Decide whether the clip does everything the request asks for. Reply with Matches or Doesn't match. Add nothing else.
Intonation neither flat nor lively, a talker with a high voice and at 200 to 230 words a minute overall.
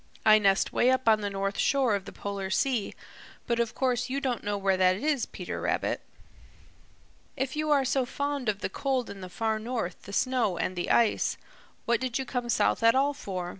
Matches